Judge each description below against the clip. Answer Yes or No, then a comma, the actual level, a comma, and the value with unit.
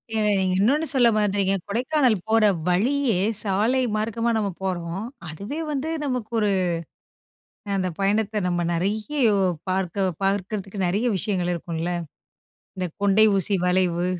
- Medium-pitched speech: No, high, 200 Hz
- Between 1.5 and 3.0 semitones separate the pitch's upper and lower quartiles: No, average, 3.4 semitones